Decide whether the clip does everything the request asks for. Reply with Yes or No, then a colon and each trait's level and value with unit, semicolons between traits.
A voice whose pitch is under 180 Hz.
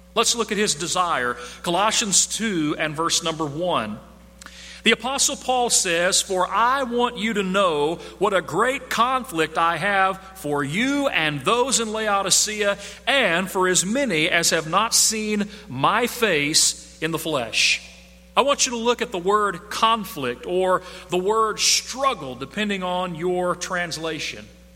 No: high, 190 Hz